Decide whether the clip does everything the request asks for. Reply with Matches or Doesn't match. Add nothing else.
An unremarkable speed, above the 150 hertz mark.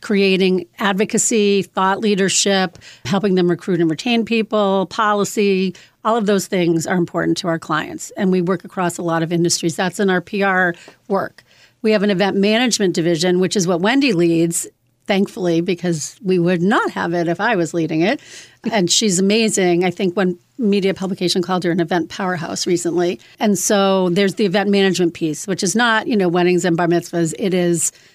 Matches